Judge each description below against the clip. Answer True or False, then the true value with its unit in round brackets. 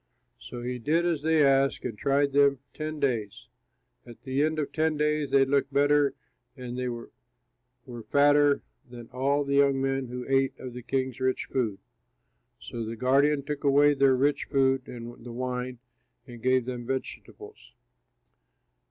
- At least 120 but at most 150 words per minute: False (160 wpm)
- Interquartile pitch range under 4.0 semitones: True (2.4 semitones)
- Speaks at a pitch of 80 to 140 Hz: True (135 Hz)